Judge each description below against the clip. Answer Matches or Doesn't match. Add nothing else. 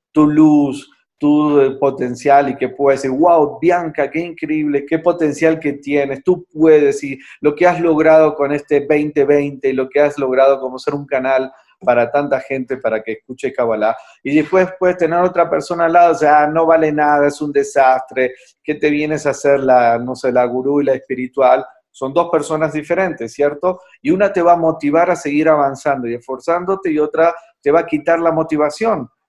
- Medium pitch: Matches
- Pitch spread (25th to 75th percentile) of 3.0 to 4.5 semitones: Matches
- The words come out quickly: Matches